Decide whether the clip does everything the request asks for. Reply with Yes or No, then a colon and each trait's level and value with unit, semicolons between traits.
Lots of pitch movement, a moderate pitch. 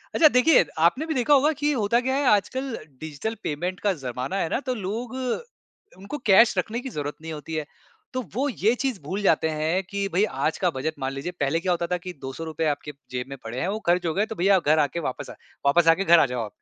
Yes: wide, 6.8 semitones; medium, 180 Hz